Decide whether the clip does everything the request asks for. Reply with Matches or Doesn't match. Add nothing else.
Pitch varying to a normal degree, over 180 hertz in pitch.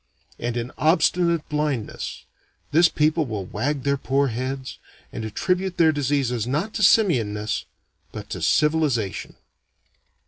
Doesn't match